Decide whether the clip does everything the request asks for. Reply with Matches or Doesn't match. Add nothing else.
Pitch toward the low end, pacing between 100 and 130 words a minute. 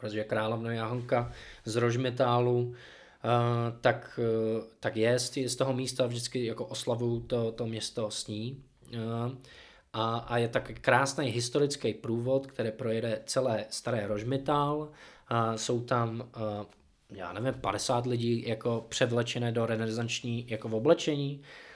Matches